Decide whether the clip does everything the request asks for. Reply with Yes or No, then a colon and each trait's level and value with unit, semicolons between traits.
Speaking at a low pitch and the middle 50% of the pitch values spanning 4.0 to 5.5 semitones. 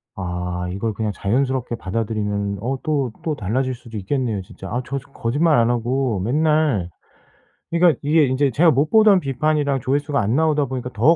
Yes: low, 130 Hz; average, 5.1 semitones